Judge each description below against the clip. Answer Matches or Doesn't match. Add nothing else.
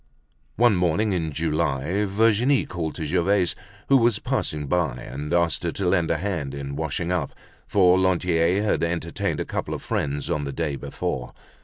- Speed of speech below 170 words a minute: Doesn't match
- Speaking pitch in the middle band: Doesn't match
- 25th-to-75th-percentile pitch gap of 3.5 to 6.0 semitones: Matches